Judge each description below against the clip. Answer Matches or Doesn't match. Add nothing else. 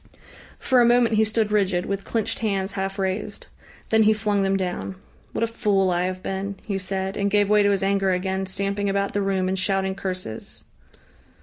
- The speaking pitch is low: Doesn't match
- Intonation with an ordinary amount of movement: Doesn't match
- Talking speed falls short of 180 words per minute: Doesn't match